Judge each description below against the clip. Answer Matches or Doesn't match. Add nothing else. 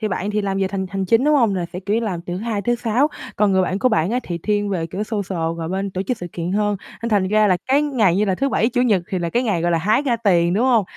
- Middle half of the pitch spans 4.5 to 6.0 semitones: Doesn't match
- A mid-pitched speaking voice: Doesn't match